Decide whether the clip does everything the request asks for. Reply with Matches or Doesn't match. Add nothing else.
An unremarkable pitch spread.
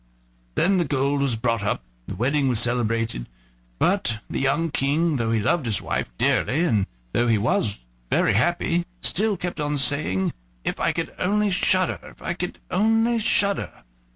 Doesn't match